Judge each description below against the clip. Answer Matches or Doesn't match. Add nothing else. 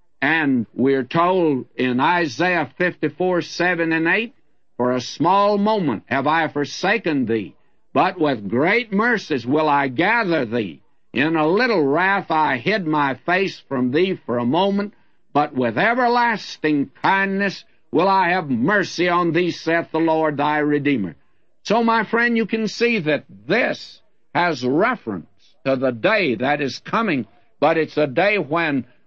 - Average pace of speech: Matches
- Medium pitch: Matches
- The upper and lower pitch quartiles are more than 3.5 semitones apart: Matches